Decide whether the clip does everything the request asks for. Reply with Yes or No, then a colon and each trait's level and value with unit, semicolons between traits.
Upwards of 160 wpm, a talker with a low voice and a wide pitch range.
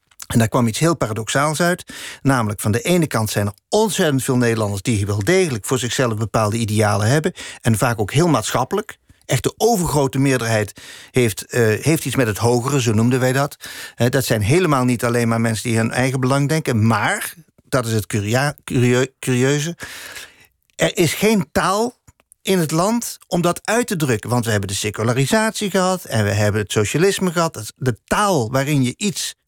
Yes: average, 190 wpm; low, 130 Hz; wide, 6.2 semitones